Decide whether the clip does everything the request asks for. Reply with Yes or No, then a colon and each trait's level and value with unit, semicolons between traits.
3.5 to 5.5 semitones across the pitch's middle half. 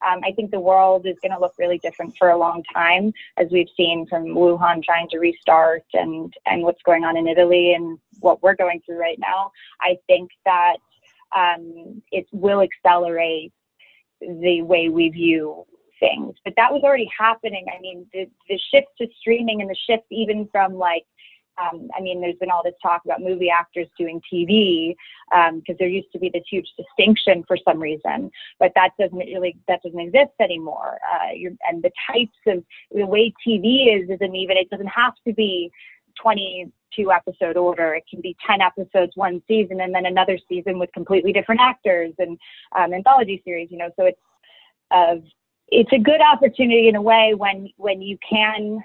No: average, 3.0 semitones